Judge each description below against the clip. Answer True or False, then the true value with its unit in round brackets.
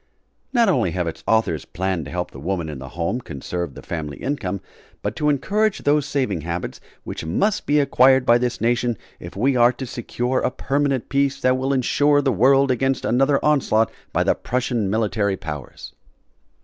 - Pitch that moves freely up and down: True (7.1 semitones)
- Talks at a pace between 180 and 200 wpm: True (185 wpm)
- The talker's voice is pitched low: True (120 Hz)